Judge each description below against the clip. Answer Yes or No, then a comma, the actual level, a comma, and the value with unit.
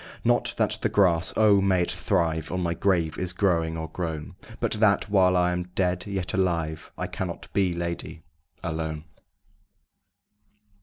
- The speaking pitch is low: Yes, very low, 90 Hz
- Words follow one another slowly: No, average, 155 wpm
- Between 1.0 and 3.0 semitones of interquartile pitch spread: Yes, average, 2.7 semitones